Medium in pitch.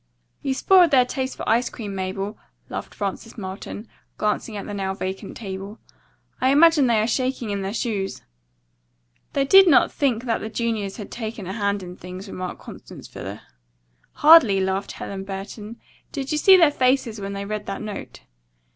No: high, 215 Hz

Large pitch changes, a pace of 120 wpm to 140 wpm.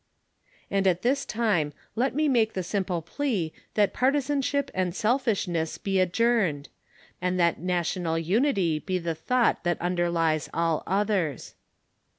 Yes: wide, 5.7 semitones; slow, 135 wpm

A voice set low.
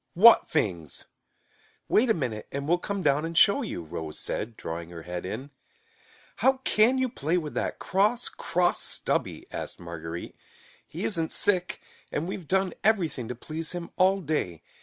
No: medium, 160 Hz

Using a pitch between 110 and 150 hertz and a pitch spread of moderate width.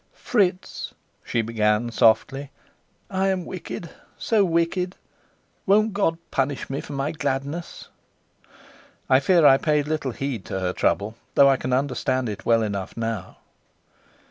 No: medium, 140 Hz; wide, 6.6 semitones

